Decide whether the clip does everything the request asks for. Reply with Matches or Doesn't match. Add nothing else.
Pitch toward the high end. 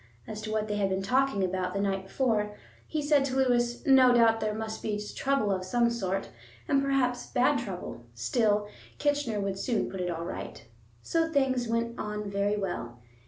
Matches